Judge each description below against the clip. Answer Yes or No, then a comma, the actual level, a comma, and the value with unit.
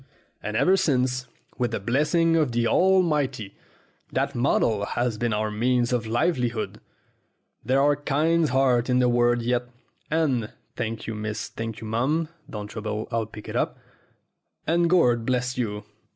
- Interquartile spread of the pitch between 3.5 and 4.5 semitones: Yes, average, 4.2 semitones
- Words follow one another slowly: No, average, 155 wpm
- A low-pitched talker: Yes, low, 120 Hz